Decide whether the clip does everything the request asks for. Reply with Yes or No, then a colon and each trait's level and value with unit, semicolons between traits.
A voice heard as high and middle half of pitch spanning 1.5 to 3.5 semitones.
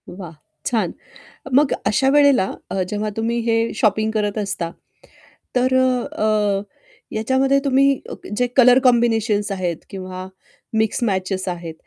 No: high, 220 Hz; average, 4.3 semitones